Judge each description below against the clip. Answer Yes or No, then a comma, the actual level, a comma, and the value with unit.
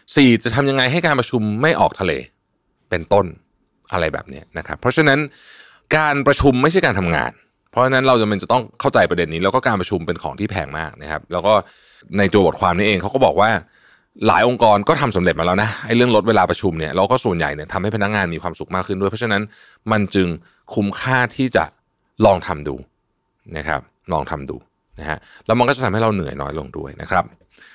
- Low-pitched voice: Yes, low, 105 Hz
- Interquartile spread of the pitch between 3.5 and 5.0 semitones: No, wide, 5.5 semitones